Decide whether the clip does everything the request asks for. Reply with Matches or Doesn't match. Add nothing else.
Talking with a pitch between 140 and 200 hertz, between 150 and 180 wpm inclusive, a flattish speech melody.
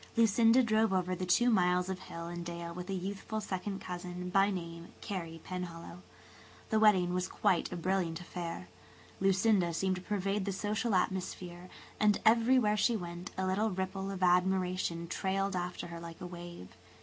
Matches